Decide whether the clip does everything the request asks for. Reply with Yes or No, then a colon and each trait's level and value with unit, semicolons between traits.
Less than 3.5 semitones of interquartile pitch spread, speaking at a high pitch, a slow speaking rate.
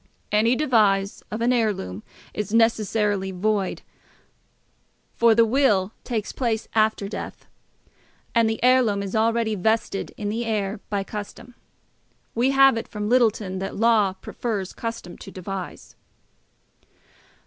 Yes: average, 2.7 semitones; high, 215 Hz; slow, 125 wpm